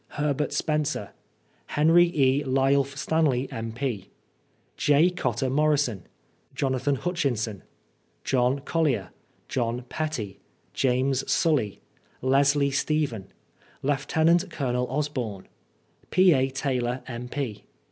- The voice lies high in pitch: No, low, 135 Hz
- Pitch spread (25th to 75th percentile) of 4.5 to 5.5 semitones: No, average, 3.3 semitones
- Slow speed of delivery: Yes, slow, 90 wpm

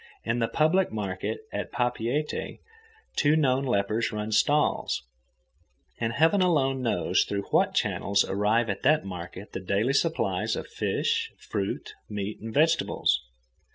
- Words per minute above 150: No, slow, 135 wpm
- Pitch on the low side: Yes, low, 115 Hz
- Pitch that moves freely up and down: Yes, wide, 6.7 semitones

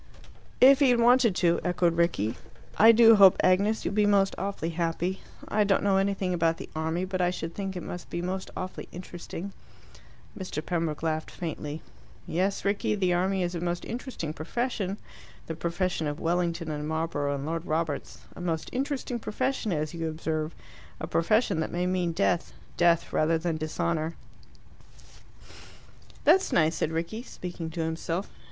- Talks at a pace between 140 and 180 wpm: Yes, average, 165 wpm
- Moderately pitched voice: Yes, medium, 175 Hz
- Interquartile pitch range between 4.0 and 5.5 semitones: No, average, 3.3 semitones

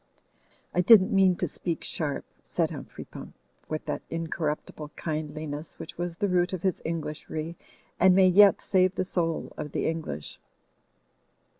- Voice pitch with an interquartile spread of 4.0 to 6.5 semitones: No, average, 3.0 semitones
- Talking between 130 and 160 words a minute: Yes, average, 150 wpm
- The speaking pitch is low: No, medium, 165 Hz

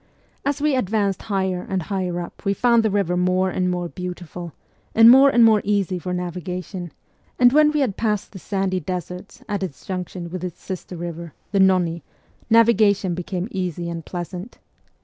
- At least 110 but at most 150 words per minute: No, average, 175 wpm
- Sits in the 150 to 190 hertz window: Yes, medium, 185 Hz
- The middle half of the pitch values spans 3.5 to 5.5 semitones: No, average, 2.8 semitones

